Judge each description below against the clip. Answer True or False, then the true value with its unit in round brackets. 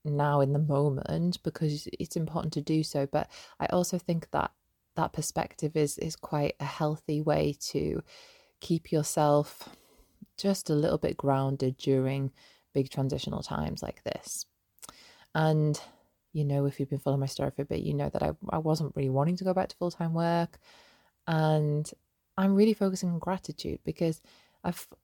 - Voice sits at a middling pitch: True (155 Hz)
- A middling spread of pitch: True (3.3 semitones)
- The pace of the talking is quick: False (175 wpm)